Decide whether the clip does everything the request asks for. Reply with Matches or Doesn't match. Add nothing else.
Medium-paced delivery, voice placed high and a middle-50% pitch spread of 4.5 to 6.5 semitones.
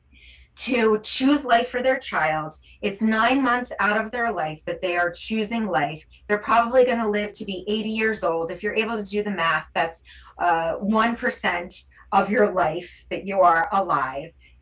Matches